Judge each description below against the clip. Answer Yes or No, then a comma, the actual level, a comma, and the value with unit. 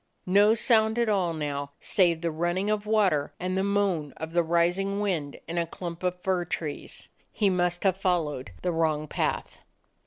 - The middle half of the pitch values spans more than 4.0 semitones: No, average, 3.4 semitones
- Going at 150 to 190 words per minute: Yes, average, 180 wpm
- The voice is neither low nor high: Yes, medium, 175 Hz